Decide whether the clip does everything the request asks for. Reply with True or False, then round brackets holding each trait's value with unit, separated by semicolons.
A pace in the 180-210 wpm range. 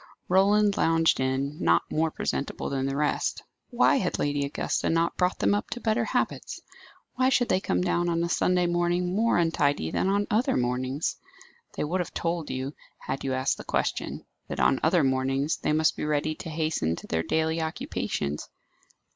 True (185 wpm)